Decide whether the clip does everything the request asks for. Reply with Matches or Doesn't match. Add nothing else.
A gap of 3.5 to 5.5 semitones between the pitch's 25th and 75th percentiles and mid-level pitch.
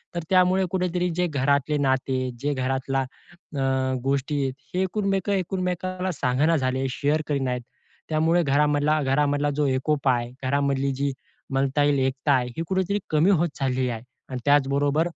Matches